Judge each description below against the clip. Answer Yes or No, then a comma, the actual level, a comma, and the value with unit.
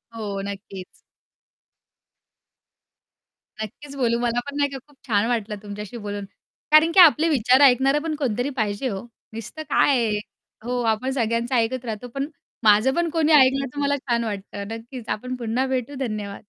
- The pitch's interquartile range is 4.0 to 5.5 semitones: Yes, average, 4.3 semitones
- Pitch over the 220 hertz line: Yes, high, 245 Hz